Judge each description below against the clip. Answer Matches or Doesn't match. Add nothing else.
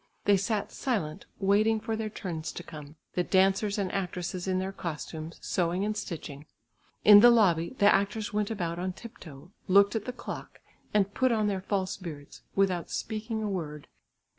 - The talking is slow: Doesn't match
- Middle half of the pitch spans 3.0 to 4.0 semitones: Matches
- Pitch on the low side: Doesn't match